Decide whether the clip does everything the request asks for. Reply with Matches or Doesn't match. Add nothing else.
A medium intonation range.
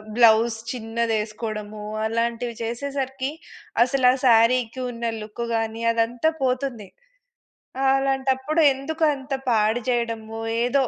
Matches